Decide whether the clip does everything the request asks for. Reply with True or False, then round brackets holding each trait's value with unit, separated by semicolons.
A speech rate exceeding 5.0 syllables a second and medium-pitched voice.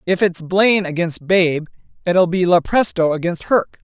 False (4.5 syllables/s; 175 Hz)